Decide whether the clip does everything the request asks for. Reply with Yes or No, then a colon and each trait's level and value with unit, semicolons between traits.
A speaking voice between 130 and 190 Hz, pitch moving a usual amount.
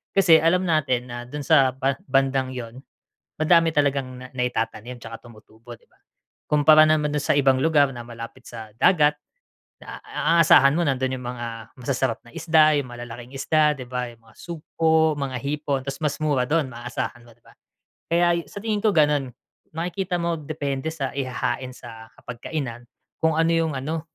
Yes: medium, 140 Hz; average, 4.2 semitones